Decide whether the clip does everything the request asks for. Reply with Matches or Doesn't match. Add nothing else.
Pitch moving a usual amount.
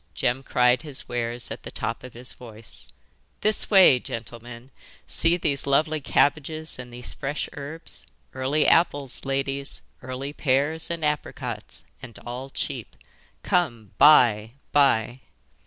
Matches